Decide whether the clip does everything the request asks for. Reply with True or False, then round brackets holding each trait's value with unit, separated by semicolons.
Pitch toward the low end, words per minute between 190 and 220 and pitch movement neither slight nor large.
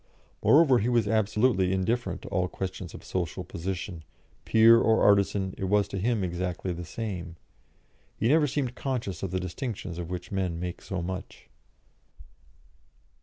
False (95 Hz; 155 wpm; 3.8 semitones)